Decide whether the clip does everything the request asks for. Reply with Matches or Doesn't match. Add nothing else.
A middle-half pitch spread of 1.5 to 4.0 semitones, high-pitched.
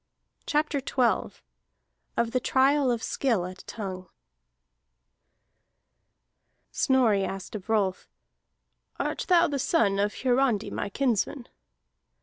Doesn't match